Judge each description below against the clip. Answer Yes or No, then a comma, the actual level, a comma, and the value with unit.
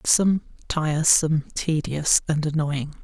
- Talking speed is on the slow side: Yes, slow, 100 wpm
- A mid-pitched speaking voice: Yes, medium, 155 Hz